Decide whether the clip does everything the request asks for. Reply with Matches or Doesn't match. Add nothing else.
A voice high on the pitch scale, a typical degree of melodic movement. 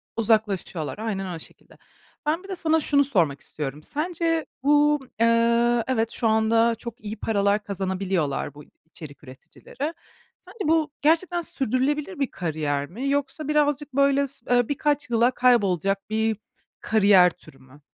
Doesn't match